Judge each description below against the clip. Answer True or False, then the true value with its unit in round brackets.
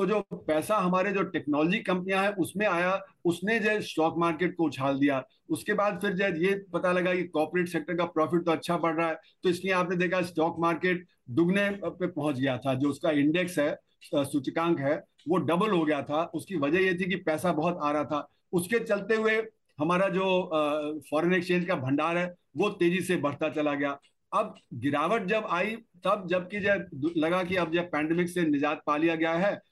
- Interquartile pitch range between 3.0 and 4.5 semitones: True (3.4 semitones)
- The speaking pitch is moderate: True (175 Hz)